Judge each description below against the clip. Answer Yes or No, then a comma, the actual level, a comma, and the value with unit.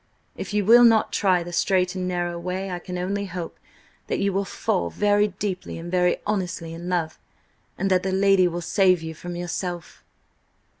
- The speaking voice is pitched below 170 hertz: No, medium, 180 Hz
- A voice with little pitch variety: Yes, narrow, 2.0 semitones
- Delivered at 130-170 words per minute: No, average, 190 wpm